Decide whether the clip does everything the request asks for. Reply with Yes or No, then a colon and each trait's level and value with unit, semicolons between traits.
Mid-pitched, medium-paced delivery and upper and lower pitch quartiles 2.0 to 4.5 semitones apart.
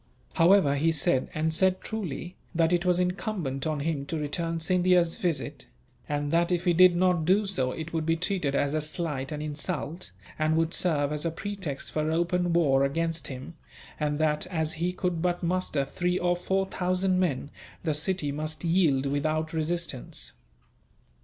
Yes: medium, 165 Hz; average, 175 wpm; average, 3.0 semitones